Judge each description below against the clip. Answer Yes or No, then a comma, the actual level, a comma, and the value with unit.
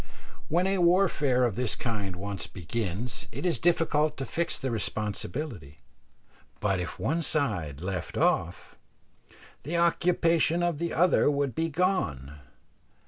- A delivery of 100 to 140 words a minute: Yes, slow, 135 wpm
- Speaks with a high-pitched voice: No, low, 135 Hz